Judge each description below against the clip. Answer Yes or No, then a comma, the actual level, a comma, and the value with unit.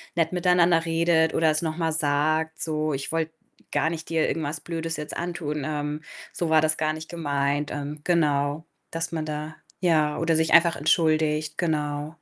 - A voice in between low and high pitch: Yes, medium, 155 Hz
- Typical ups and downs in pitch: No, narrow, 1.6 semitones